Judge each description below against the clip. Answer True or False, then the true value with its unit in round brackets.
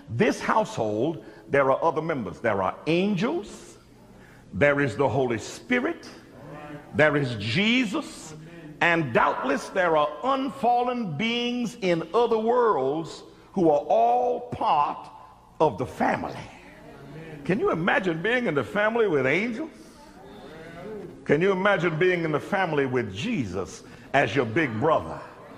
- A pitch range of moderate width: False (7.6 semitones)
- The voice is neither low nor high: True (180 Hz)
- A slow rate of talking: True (130 wpm)